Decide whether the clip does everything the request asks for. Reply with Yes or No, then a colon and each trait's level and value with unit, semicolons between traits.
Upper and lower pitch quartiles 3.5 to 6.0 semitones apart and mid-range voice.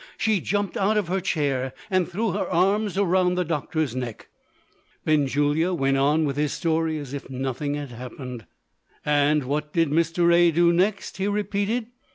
Yes: average, 4.6 semitones; medium, 160 Hz